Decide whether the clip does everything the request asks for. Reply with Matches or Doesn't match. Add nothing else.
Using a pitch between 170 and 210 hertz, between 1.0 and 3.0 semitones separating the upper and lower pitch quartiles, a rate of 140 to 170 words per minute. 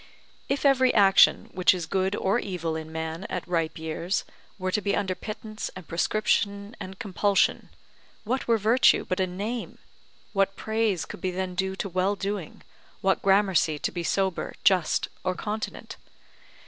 Matches